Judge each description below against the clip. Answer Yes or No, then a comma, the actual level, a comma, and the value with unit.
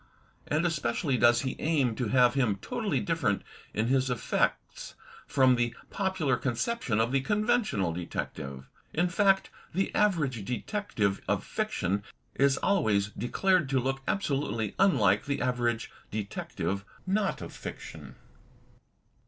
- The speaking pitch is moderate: No, low, 130 Hz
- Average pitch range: No, wide, 7.7 semitones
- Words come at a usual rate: No, slow, 130 wpm